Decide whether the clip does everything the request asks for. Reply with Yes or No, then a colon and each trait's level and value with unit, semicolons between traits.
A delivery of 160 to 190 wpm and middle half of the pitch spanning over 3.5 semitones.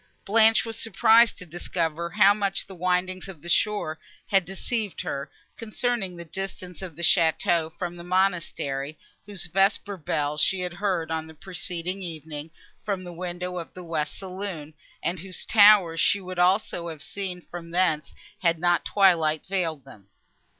No: average, 165 wpm; average, 2.9 semitones